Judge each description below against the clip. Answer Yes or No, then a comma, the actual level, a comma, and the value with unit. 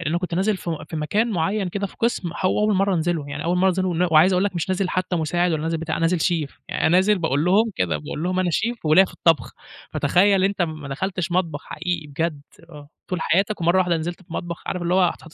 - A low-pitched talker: No, medium, 175 Hz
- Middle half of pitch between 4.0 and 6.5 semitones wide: No, average, 2.7 semitones